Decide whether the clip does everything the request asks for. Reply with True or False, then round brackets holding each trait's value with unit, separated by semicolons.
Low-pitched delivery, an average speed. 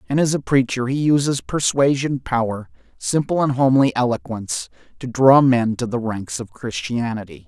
True (130 Hz; 160 wpm)